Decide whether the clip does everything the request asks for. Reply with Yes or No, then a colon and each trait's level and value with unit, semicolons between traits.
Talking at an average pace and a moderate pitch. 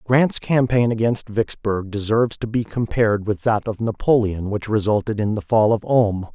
No: average, 180 wpm; low, 110 Hz